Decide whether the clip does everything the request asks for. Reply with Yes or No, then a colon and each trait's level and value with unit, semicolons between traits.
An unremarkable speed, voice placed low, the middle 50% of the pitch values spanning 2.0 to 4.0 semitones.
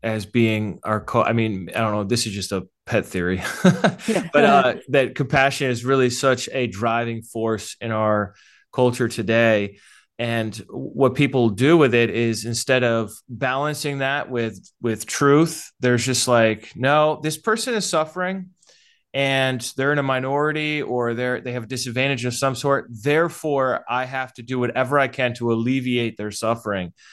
Yes: average, 170 wpm; low, 125 Hz; average, 3.5 semitones